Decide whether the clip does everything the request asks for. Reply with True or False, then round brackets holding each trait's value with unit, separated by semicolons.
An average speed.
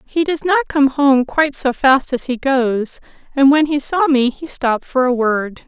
False (220 wpm)